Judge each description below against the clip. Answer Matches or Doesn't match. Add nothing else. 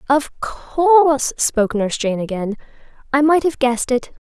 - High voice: Matches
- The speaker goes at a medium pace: Matches